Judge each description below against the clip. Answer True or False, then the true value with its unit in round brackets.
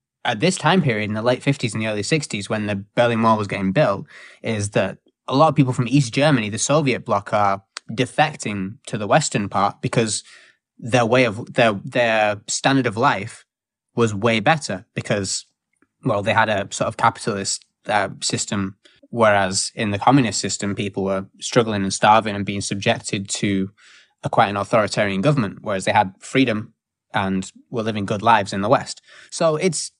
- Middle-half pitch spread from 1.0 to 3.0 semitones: False (4.2 semitones)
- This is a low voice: True (110 Hz)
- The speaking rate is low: False (185 wpm)